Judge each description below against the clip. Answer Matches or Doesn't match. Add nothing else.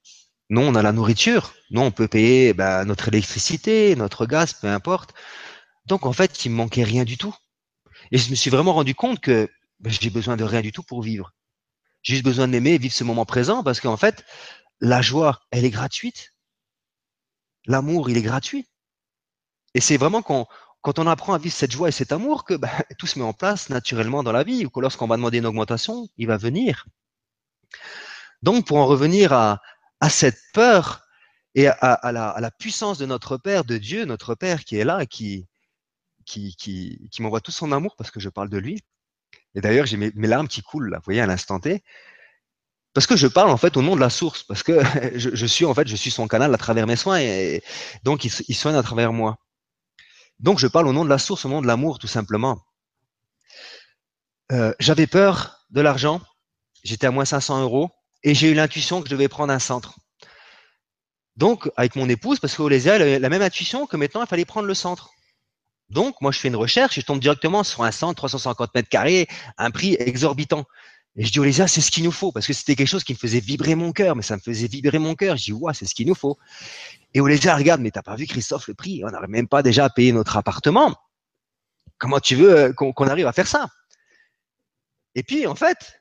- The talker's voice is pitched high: Doesn't match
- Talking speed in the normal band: Doesn't match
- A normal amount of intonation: Doesn't match